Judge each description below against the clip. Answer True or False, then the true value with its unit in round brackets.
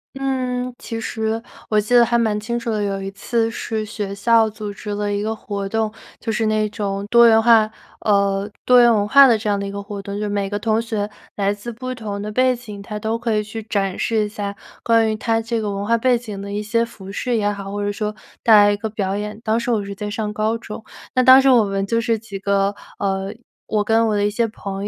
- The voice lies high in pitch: True (215 Hz)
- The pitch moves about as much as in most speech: False (2.1 semitones)